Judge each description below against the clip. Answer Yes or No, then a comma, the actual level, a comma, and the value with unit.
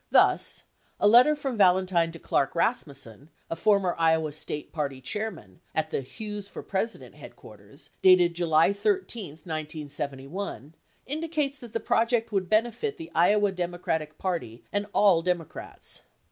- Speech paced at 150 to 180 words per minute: No, average, 140 wpm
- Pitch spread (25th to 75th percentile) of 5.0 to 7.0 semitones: Yes, wide, 5.6 semitones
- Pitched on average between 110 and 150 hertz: No, medium, 185 Hz